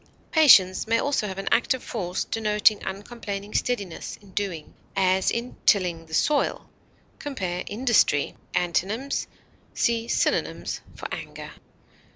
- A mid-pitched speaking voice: No, high, 205 Hz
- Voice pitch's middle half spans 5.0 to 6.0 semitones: No, average, 4.0 semitones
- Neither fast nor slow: No, slow, 120 wpm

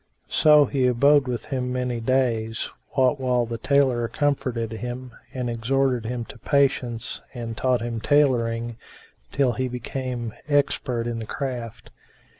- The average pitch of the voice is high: No, low, 125 Hz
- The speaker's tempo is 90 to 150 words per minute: Yes, average, 140 wpm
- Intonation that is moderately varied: No, narrow, 2.3 semitones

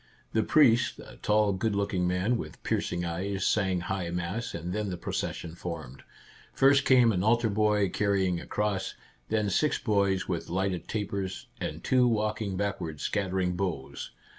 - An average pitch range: Yes, average, 3.0 semitones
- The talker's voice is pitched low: Yes, low, 100 Hz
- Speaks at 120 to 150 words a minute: No, average, 160 wpm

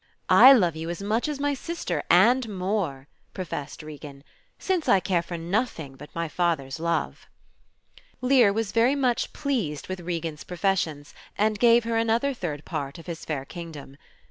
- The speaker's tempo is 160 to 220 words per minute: Yes, average, 165 wpm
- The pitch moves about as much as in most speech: No, wide, 6.5 semitones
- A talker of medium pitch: Yes, medium, 180 Hz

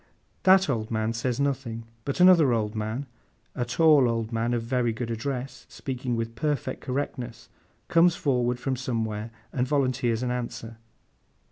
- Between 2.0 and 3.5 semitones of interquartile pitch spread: Yes, average, 2.8 semitones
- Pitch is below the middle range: Yes, low, 125 Hz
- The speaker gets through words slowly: No, average, 150 wpm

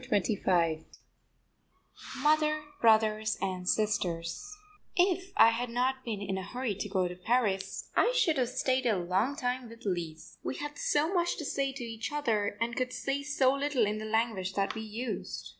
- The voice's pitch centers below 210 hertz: No, high, 230 Hz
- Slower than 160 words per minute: No, average, 180 wpm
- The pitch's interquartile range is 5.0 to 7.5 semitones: Yes, wide, 5.5 semitones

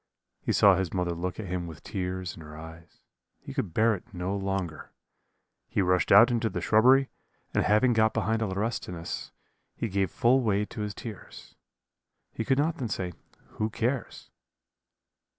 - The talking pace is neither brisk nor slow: Yes, average, 170 wpm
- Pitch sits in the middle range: No, low, 100 Hz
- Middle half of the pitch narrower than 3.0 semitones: No, average, 4.0 semitones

